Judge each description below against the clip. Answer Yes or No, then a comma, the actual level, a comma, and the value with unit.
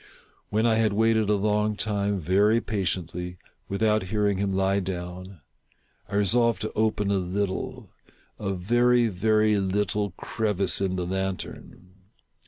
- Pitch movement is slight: Yes, narrow, 2.3 semitones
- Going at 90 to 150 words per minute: Yes, average, 140 wpm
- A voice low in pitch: Yes, low, 100 Hz